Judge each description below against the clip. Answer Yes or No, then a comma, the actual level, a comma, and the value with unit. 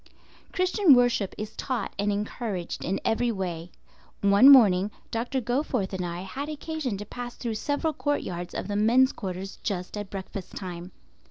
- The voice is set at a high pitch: Yes, high, 210 Hz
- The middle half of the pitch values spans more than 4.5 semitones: Yes, average, 5.2 semitones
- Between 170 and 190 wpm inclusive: No, average, 160 wpm